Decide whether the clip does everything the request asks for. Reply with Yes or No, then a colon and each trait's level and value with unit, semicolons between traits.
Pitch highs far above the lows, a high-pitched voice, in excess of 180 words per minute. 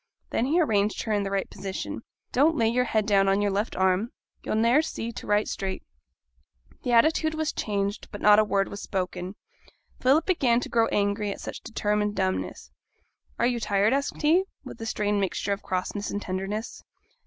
No: average, 3.1 semitones; high, 210 Hz; average, 190 wpm